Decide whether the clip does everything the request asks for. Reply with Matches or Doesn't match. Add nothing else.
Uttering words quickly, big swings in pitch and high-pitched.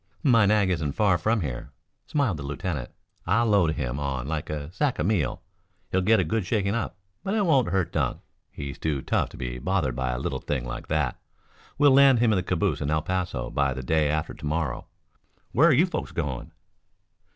Doesn't match